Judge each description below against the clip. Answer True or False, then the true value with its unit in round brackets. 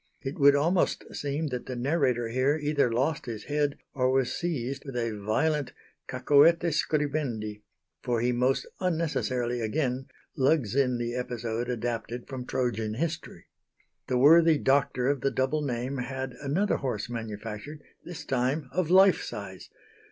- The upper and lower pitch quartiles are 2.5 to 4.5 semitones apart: True (3.5 semitones)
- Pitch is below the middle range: True (130 Hz)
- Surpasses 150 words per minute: False (145 wpm)